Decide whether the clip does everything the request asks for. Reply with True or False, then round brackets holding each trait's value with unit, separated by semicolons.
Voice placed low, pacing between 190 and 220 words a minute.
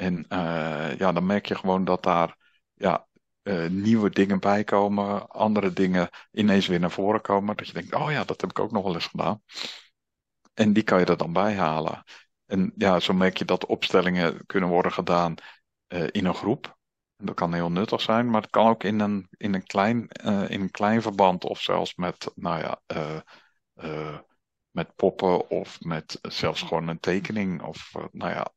True (95 Hz; 200 wpm)